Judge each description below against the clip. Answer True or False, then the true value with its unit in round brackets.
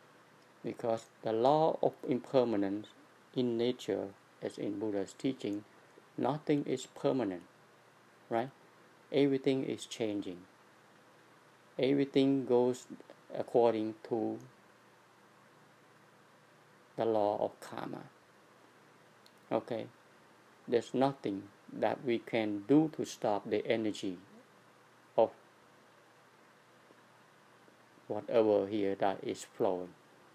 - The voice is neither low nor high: False (115 Hz)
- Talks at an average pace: False (85 wpm)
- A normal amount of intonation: True (4.3 semitones)